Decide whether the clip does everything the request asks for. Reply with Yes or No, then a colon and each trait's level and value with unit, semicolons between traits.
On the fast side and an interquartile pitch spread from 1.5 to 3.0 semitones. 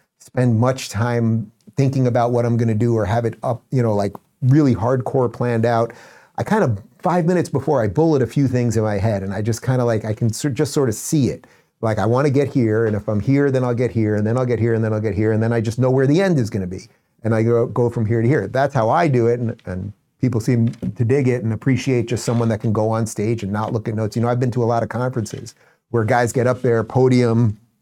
Yes: fast, 285 wpm; narrow, 2.5 semitones